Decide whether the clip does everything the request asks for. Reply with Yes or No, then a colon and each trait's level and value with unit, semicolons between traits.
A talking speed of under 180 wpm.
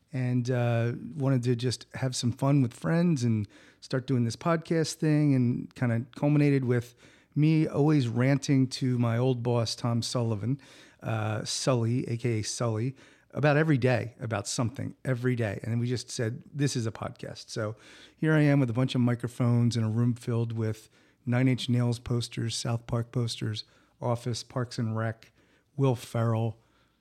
Yes: average, 170 wpm